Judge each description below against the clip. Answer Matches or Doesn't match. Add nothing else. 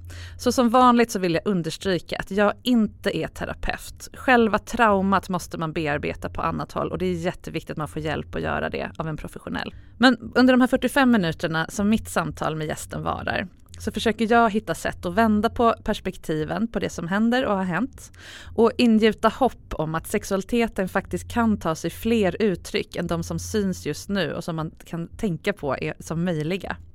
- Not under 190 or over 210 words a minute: Matches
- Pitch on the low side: Doesn't match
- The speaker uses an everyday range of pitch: Doesn't match